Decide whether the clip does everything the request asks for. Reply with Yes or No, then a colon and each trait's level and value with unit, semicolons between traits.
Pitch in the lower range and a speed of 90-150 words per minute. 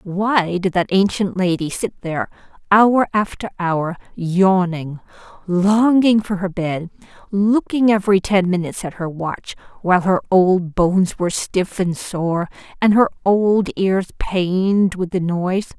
No: high, 190 Hz; average, 145 wpm